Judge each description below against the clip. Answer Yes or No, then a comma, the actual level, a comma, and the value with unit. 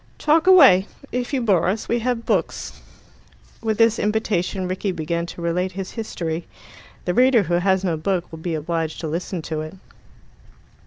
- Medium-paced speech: Yes, average, 170 wpm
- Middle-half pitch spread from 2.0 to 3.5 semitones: No, average, 4.9 semitones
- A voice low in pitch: No, medium, 185 Hz